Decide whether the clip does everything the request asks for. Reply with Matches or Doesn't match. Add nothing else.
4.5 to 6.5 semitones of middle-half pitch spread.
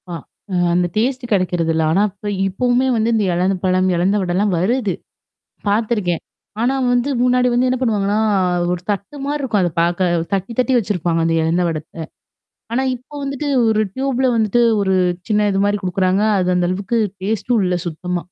Matches